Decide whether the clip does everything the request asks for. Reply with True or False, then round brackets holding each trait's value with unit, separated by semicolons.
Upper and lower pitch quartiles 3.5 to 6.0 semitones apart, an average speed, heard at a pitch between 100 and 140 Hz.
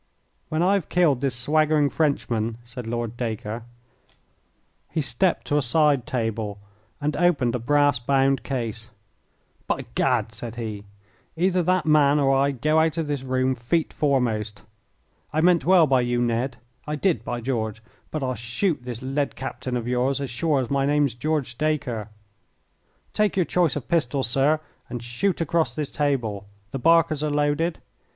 True (4.4 semitones; 165 wpm; 135 Hz)